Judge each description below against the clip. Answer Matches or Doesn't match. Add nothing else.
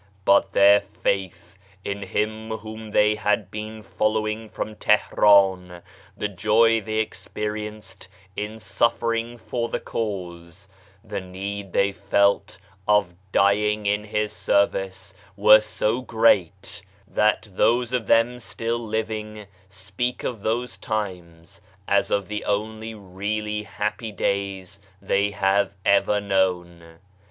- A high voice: Doesn't match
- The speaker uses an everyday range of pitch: Doesn't match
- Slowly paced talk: Matches